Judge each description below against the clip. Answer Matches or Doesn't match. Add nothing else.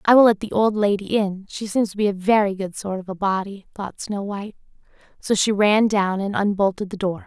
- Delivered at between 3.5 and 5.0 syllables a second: Doesn't match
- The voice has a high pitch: Matches